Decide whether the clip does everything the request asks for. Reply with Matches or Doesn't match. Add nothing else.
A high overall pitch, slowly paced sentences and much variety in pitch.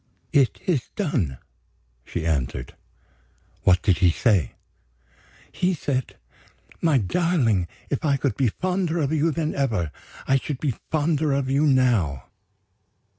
Doesn't match